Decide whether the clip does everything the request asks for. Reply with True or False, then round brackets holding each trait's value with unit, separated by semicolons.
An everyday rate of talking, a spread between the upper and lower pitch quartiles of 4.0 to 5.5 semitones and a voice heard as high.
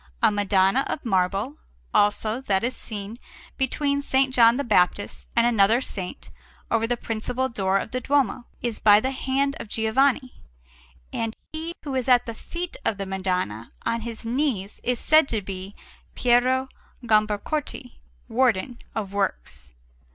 True (150 wpm; 4.4 semitones; 230 Hz)